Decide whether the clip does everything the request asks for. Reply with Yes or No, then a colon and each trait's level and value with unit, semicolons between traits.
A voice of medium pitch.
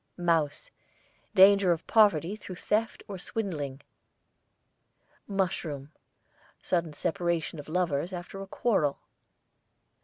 Yes: medium, 175 Hz